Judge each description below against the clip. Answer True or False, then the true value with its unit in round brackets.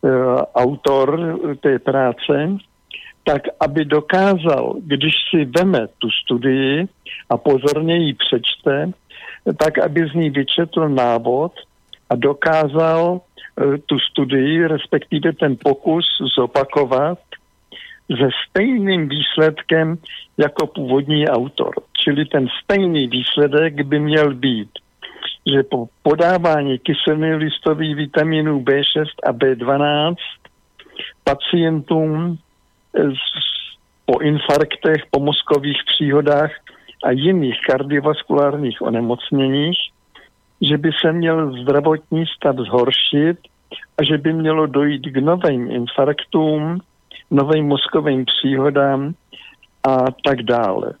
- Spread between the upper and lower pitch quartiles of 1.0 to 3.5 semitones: True (2.7 semitones)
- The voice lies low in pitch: False (150 Hz)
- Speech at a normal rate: False (100 wpm)